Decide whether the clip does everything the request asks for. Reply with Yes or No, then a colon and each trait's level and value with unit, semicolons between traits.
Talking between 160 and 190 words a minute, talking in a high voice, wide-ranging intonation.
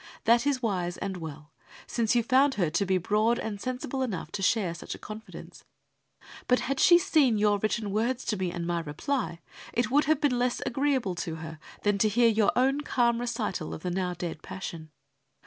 No: average, 200 wpm; high, 215 Hz; wide, 5.7 semitones